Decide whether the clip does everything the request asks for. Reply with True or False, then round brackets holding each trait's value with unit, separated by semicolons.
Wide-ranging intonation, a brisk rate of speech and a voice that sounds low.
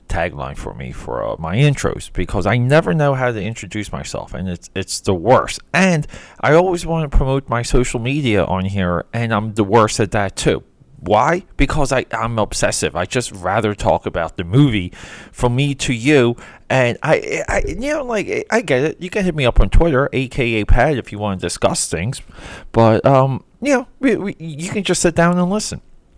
True (7.2 semitones; 210 wpm; 125 Hz)